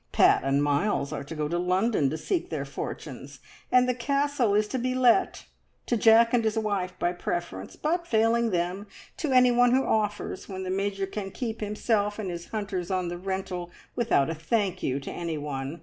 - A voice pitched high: Yes, high, 200 Hz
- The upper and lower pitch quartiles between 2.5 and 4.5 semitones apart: No, average, 5.2 semitones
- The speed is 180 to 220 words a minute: Yes, average, 195 wpm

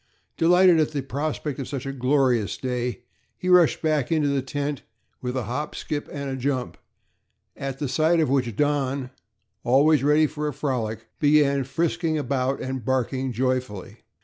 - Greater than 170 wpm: No, average, 160 wpm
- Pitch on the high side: No, medium, 140 Hz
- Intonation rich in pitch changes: No, average, 2.8 semitones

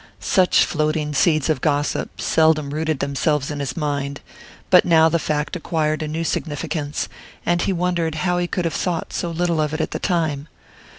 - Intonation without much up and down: Yes, narrow, 2.3 semitones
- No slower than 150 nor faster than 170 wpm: No, average, 185 wpm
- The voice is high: No, medium, 155 Hz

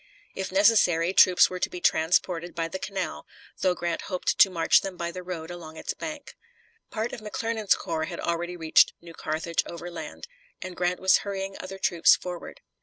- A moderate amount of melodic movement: No, narrow, 2.2 semitones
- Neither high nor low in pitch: Yes, medium, 180 Hz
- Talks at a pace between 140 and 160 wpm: No, average, 180 wpm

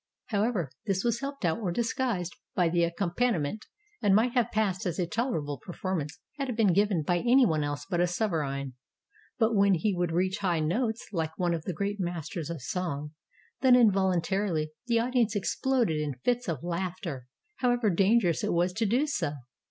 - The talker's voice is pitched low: No, medium, 185 Hz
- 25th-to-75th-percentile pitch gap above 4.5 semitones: Yes, average, 5.0 semitones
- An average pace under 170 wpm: No, average, 185 wpm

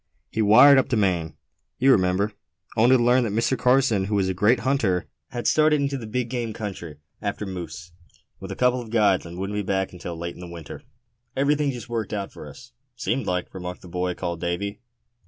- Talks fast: Yes, fast, 210 wpm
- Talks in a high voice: No, low, 105 Hz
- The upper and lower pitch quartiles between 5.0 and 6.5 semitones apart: Yes, wide, 5.5 semitones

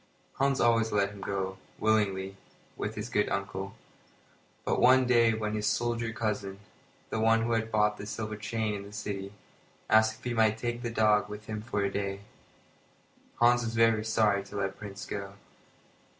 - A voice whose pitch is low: Yes, low, 110 Hz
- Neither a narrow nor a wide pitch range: No, narrow, 2.0 semitones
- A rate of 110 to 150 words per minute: No, average, 180 wpm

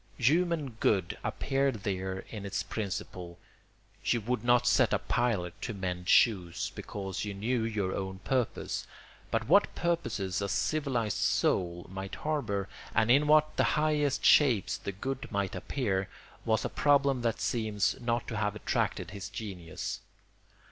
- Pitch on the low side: Yes, low, 110 Hz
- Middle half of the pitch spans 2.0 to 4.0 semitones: No, average, 5.2 semitones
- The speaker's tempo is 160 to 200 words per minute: No, average, 145 wpm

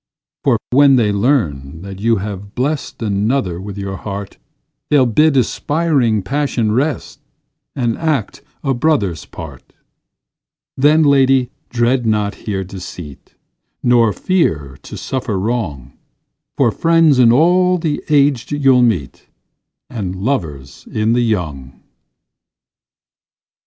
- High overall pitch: No, low, 115 Hz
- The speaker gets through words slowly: Yes, slow, 115 wpm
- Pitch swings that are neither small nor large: No, wide, 6.0 semitones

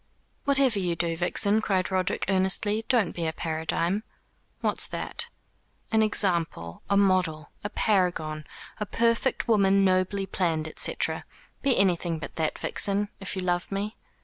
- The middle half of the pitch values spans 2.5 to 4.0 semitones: Yes, average, 3.3 semitones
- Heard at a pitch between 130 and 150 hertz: No, high, 190 Hz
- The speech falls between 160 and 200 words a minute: No, average, 145 wpm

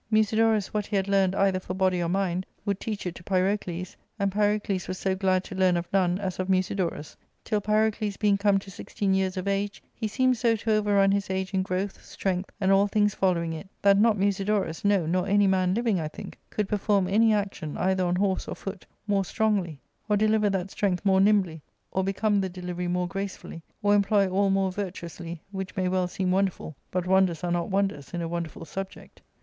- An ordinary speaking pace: No, fast, 210 wpm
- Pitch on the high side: Yes, high, 195 Hz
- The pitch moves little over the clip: Yes, narrow, 1.9 semitones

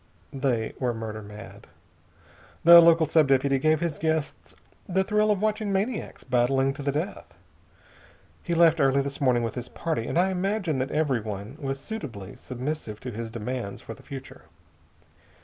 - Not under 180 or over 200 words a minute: No, average, 165 wpm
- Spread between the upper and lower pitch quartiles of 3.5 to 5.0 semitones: No, wide, 5.5 semitones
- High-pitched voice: No, medium, 140 Hz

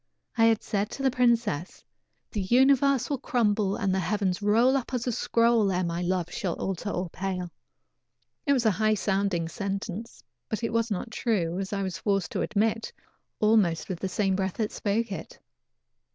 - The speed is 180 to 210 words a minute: Yes, average, 185 wpm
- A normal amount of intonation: Yes, average, 3.4 semitones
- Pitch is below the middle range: No, high, 205 Hz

